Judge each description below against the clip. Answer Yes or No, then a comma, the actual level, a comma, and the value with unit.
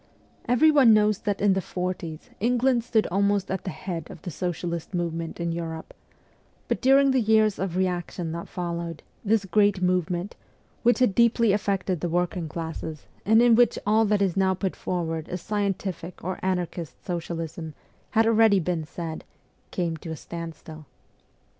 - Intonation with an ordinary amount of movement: Yes, average, 3.8 semitones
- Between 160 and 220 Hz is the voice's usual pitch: Yes, medium, 185 Hz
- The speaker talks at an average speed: Yes, average, 160 wpm